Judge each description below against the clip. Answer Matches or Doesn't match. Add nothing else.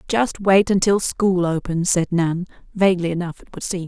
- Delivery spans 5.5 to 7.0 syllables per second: Doesn't match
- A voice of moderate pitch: Matches